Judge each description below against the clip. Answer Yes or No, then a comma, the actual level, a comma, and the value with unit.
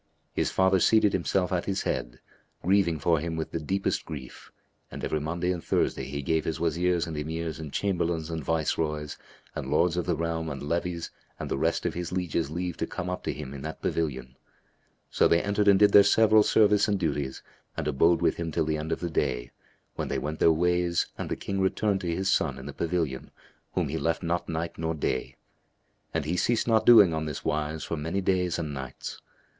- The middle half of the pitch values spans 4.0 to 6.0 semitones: No, average, 2.8 semitones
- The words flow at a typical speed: No, fast, 215 wpm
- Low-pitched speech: Yes, very low, 85 Hz